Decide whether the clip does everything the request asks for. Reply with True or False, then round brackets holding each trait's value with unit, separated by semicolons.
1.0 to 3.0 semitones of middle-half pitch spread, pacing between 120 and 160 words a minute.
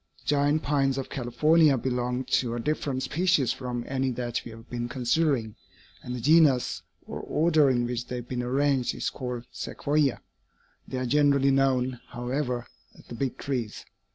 False (2.7 semitones; 170 wpm)